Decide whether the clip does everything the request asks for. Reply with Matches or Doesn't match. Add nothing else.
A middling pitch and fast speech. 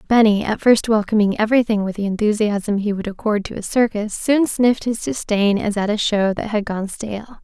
Doesn't match